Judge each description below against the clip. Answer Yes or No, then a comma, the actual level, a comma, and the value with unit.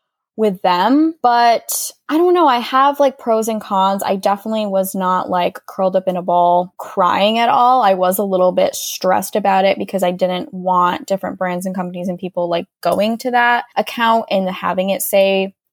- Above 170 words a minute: Yes, average, 200 wpm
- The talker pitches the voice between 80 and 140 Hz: No, high, 195 Hz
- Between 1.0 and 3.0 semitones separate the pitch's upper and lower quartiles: No, average, 3.7 semitones